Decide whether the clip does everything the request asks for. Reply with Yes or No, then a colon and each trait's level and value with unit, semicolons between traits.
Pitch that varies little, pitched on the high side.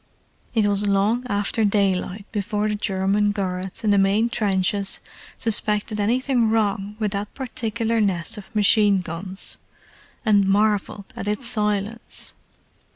Yes: narrow, 1.7 semitones; high, 205 Hz